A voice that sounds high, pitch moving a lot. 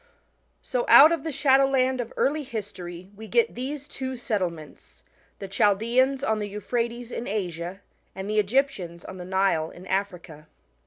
Yes: high, 215 Hz; wide, 5.8 semitones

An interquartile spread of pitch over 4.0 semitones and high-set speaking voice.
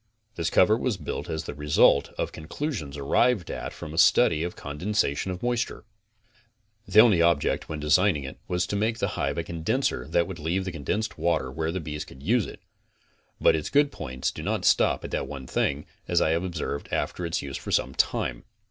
No: wide, 5.5 semitones; very low, 85 Hz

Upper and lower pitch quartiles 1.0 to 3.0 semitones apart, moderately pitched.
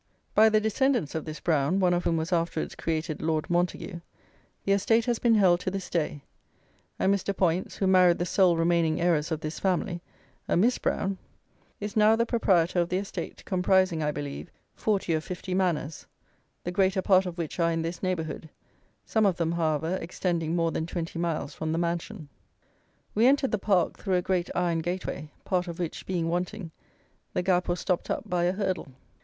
Yes: narrow, 2.6 semitones; medium, 175 Hz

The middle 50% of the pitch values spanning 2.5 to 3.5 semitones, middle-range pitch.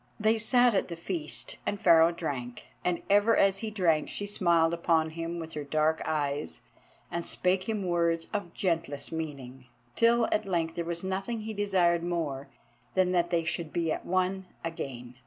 Yes: average, 3.1 semitones; medium, 170 Hz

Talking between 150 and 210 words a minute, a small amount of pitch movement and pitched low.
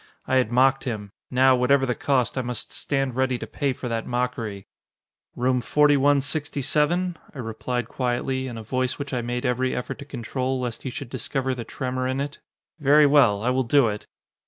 Yes: average, 190 wpm; narrow, 2.1 semitones; low, 130 Hz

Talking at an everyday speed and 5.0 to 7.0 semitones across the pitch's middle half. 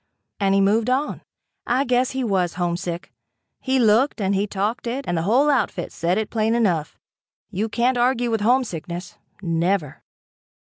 Yes: average, 160 wpm; average, 5.3 semitones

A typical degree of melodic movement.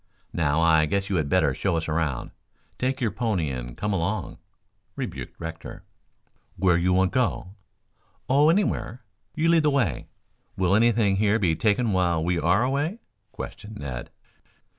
No: wide, 6.1 semitones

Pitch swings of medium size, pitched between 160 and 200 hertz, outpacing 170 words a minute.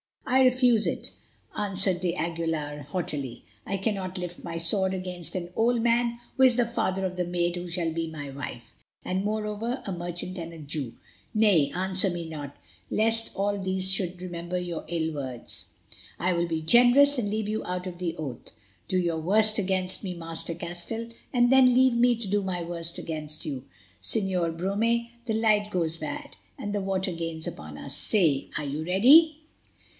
Yes: average, 4.3 semitones; medium, 185 Hz; average, 180 wpm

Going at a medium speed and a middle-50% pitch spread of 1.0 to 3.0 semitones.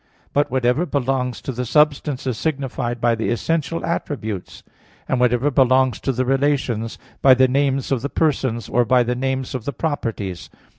Yes: average, 170 wpm; narrow, 2.5 semitones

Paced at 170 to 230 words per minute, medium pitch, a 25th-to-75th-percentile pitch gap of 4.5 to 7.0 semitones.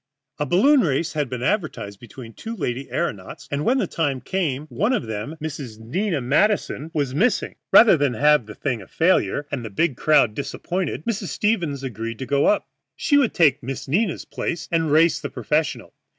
Yes: average, 190 wpm; medium, 150 Hz; wide, 5.5 semitones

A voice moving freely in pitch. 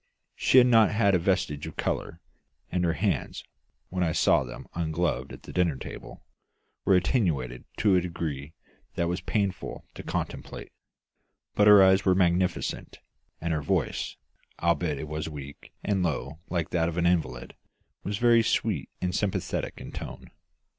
No: average, 3.3 semitones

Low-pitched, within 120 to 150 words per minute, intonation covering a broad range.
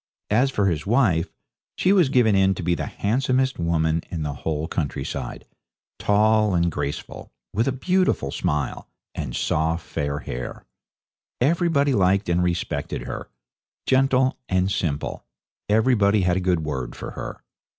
Yes: very low, 95 Hz; average, 145 wpm; wide, 7.6 semitones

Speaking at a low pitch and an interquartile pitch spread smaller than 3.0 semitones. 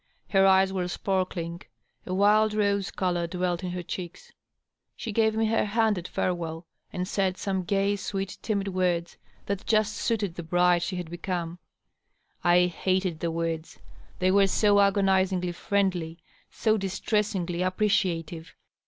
No: medium, 185 Hz; narrow, 2.4 semitones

